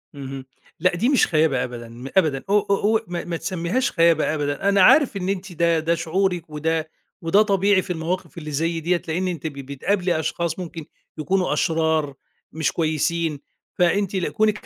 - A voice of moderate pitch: Yes, medium, 170 Hz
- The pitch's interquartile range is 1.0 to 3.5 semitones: Yes, average, 3.2 semitones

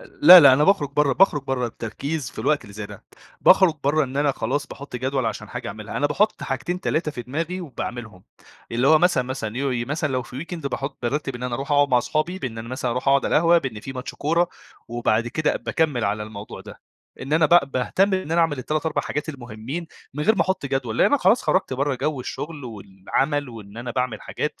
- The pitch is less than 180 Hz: Yes, low, 135 Hz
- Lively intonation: No, average, 4.3 semitones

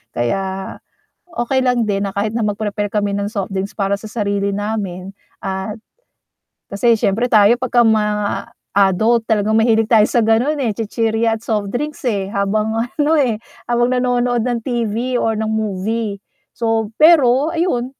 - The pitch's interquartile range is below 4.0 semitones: Yes, average, 3.0 semitones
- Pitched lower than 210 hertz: No, high, 220 Hz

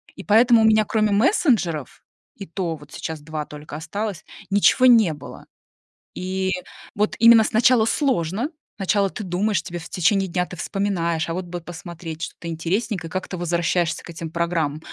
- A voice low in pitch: No, medium, 185 Hz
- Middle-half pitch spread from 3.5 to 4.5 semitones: Yes, average, 4.2 semitones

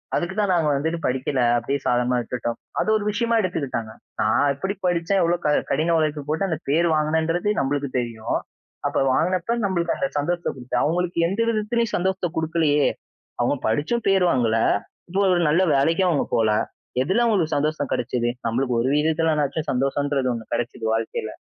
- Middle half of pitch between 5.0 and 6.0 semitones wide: Yes, wide, 5.5 semitones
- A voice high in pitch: No, medium, 155 Hz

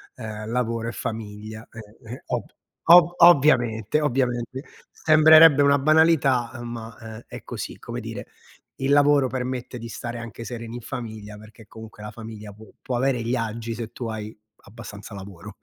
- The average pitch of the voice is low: Yes, low, 115 Hz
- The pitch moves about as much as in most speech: Yes, average, 3.1 semitones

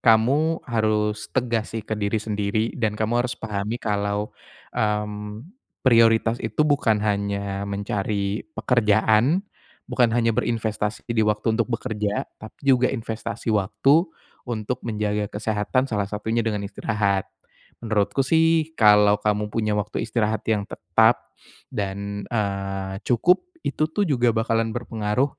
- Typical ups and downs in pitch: No, narrow, 2.2 semitones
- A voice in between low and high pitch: No, low, 110 Hz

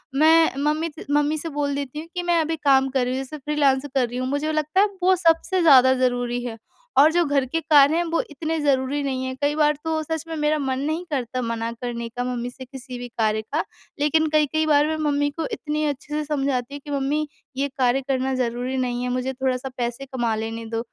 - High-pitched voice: Yes, very high, 280 Hz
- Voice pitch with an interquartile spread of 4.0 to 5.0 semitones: No, average, 3.3 semitones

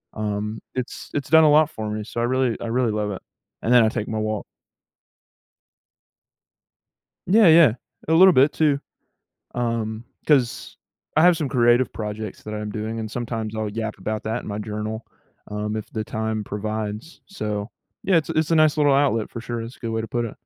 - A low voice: Yes, low, 115 Hz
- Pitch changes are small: No, average, 4.2 semitones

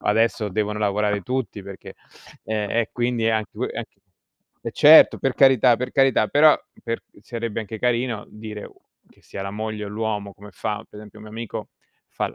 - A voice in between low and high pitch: No, low, 110 Hz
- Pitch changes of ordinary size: No, narrow, 2.2 semitones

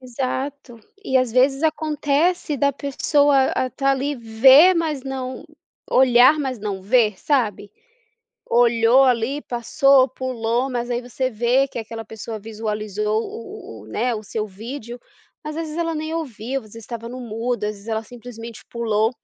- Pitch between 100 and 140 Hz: No, high, 245 Hz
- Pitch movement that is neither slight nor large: Yes, average, 3.4 semitones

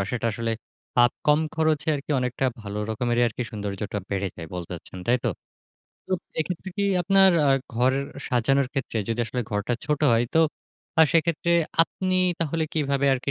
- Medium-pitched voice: No, low, 125 Hz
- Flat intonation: No, wide, 5.6 semitones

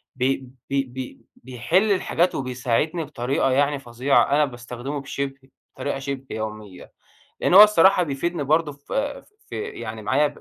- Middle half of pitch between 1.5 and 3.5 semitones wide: Yes, average, 3.2 semitones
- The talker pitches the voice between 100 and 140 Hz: Yes, low, 135 Hz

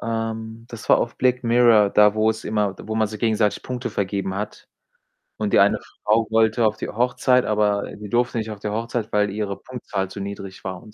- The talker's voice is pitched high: No, low, 110 Hz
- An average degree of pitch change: No, narrow, 1.9 semitones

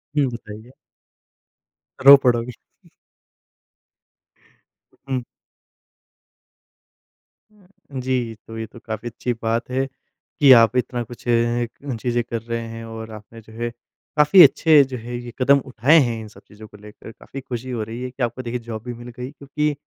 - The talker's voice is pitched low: Yes, low, 120 Hz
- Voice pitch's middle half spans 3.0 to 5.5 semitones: No, narrow, 2.4 semitones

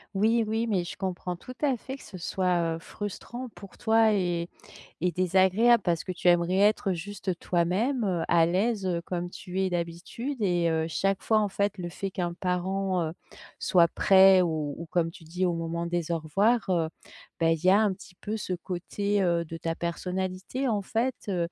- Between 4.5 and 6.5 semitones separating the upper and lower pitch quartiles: No, average, 3.1 semitones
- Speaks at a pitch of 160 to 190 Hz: Yes, medium, 185 Hz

